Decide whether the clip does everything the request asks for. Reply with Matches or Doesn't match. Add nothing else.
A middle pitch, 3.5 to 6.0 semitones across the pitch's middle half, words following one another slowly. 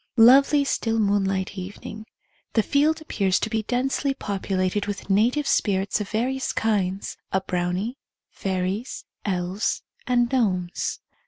Doesn't match